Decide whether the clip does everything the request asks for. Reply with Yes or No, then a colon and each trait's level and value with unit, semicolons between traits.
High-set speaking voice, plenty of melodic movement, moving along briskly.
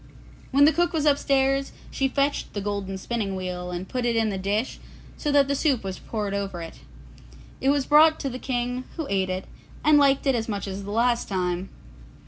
Yes: high, 235 Hz; wide, 6.1 semitones; fast, 210 wpm